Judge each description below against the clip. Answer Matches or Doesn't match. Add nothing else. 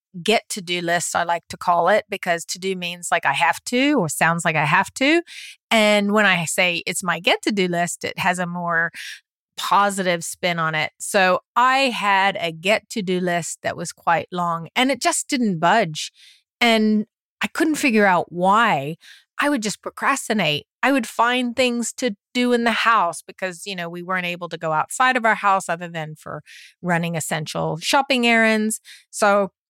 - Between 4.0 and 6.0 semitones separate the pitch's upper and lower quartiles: Matches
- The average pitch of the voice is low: Doesn't match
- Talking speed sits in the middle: Matches